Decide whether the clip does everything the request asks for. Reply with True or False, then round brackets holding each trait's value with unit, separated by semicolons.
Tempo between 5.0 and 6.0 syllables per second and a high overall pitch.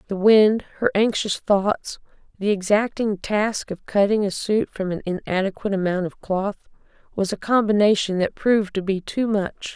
False (4.8 syllables/s; 200 Hz)